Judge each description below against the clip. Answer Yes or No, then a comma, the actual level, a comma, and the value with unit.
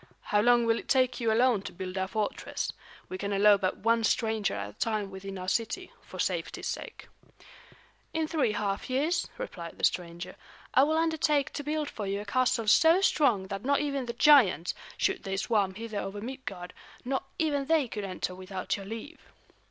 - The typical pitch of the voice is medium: No, high, 225 Hz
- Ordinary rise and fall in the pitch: No, wide, 6.0 semitones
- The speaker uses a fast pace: No, average, 190 wpm